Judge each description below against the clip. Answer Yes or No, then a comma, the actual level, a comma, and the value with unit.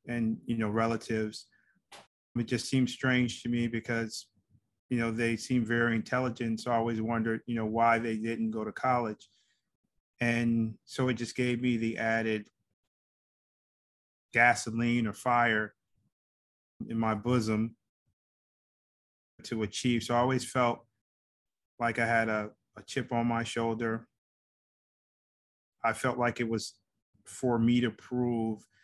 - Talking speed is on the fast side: No, average, 140 wpm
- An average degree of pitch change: No, narrow, 1.6 semitones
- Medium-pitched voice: No, low, 115 Hz